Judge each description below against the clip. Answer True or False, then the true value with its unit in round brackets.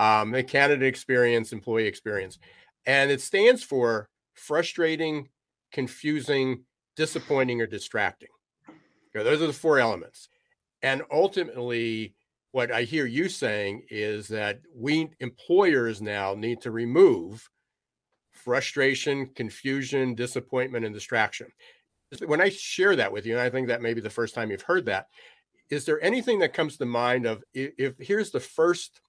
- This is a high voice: False (130 Hz)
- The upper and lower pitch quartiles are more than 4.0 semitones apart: True (4.7 semitones)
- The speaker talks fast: False (150 wpm)